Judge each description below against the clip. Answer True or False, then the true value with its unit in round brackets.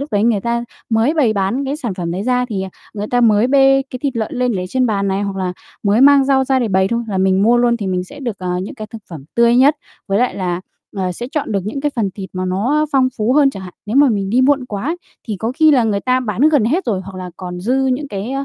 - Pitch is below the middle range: False (225 Hz)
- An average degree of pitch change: True (5.0 semitones)